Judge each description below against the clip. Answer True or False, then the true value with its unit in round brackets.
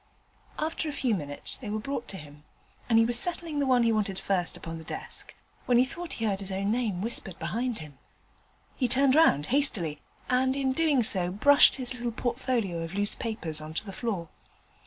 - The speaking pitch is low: False (225 Hz)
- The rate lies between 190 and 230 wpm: True (205 wpm)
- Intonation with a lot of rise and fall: True (6.0 semitones)